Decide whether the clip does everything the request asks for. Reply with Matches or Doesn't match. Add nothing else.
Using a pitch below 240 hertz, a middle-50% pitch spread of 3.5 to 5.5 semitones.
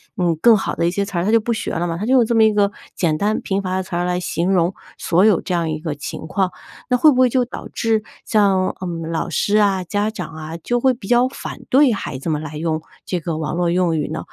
Matches